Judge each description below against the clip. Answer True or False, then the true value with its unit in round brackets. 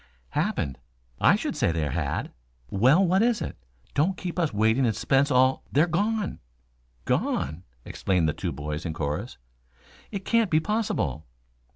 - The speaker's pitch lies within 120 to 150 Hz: True (135 Hz)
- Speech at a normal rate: True (165 wpm)